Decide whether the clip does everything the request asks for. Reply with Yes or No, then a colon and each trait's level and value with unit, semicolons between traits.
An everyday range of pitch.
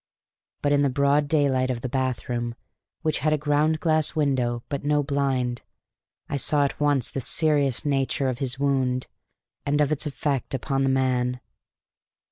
No: narrow, 2.2 semitones